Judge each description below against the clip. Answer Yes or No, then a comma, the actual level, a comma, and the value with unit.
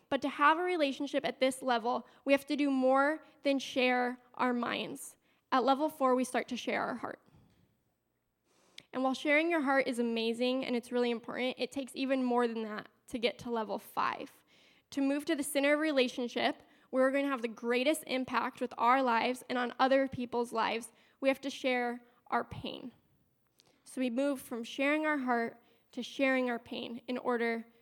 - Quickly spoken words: No, average, 195 wpm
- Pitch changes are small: Yes, narrow, 2.2 semitones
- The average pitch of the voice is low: No, very high, 255 Hz